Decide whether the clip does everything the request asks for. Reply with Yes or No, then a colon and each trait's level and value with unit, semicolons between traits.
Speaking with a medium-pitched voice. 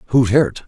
No: low, 125 Hz